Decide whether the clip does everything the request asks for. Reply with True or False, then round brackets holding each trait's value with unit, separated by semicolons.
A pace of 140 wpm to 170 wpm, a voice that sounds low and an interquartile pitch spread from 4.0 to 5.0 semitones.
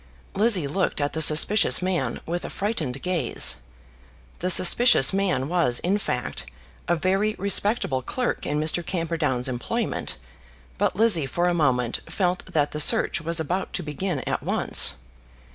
False (150 wpm; 170 Hz; 4.5 semitones)